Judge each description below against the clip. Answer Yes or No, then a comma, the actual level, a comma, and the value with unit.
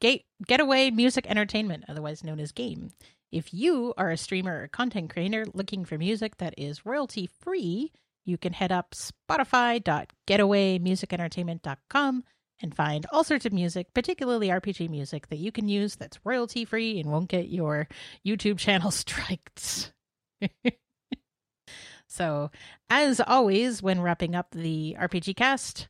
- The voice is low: No, high, 195 Hz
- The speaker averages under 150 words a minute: Yes, slow, 135 wpm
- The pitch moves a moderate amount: No, wide, 5.8 semitones